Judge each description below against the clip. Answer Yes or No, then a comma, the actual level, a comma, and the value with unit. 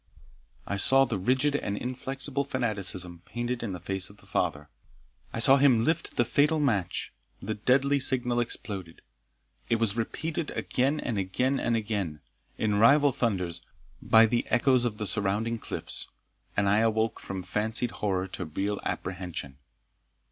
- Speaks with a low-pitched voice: Yes, low, 115 Hz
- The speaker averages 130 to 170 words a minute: Yes, average, 155 wpm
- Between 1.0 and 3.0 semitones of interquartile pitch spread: No, average, 4.8 semitones